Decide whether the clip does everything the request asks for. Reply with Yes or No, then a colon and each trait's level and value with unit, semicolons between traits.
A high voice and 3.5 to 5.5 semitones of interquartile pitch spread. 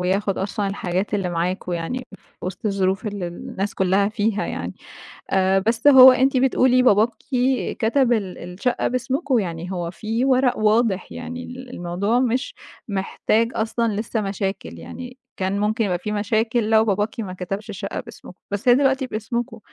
Yes: high, 215 Hz; average, 4.2 semitones